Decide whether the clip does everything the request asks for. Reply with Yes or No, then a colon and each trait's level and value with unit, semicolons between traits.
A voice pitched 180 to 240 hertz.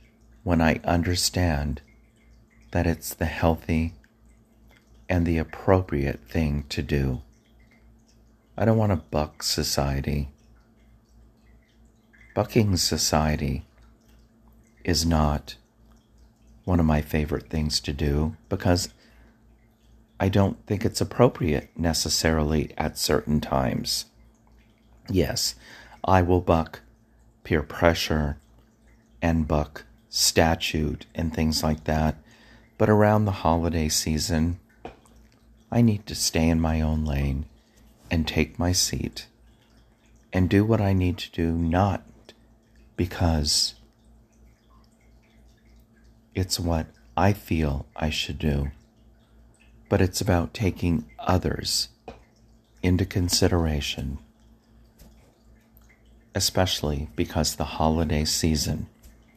No: very low, 90 Hz